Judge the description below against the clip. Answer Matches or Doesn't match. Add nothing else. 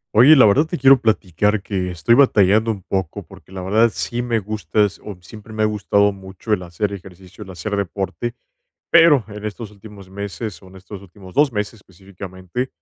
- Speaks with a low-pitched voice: Matches